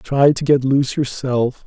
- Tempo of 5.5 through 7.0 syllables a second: No, 4.3 syllables/s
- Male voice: Yes, male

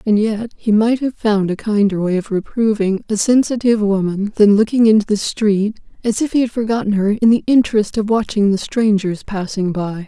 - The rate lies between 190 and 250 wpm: Yes, average, 195 wpm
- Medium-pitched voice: No, high, 210 Hz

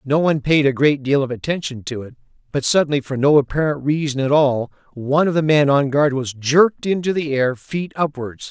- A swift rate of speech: Yes, fast, 220 wpm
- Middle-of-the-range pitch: Yes, medium, 145 Hz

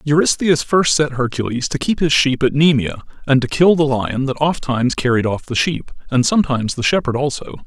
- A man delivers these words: Yes, male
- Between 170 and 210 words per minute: Yes, fast, 205 wpm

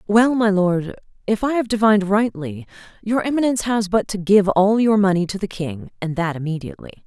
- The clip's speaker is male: No, female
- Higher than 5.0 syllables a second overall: Yes, 5.5 syllables/s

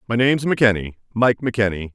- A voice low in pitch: Yes, low, 110 Hz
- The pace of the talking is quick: No, slow, 125 wpm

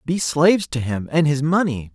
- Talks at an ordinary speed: No, fast, 215 wpm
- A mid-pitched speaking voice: Yes, medium, 150 Hz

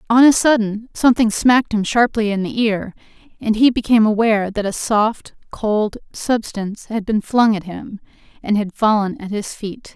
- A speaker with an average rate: Yes, average, 180 wpm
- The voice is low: No, high, 215 Hz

